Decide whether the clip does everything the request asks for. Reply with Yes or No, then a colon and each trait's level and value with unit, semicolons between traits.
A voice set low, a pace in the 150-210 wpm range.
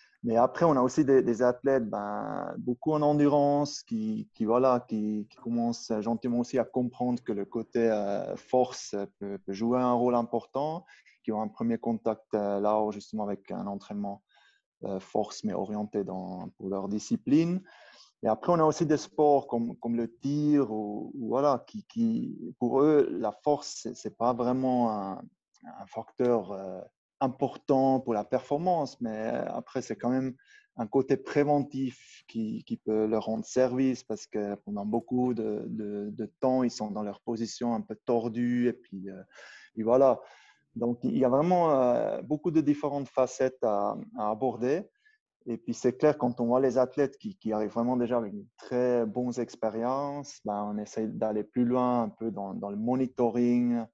Yes: low, 120 Hz; average, 180 wpm